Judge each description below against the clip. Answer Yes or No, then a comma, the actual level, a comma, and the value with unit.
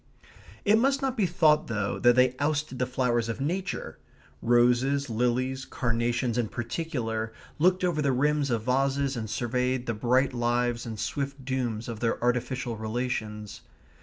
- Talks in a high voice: No, low, 125 Hz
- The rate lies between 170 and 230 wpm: No, average, 155 wpm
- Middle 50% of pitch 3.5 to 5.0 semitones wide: No, average, 3.0 semitones